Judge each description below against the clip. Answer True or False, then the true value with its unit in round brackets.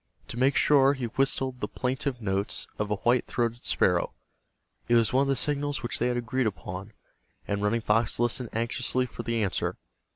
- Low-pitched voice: True (120 Hz)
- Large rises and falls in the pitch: False (2.9 semitones)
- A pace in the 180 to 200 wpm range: True (190 wpm)